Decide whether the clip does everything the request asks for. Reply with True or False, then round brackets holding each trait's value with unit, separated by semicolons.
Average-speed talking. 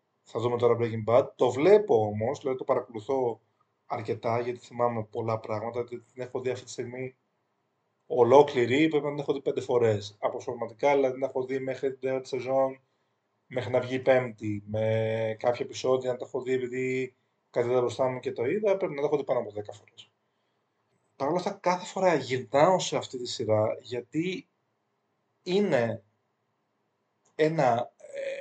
False (175 wpm)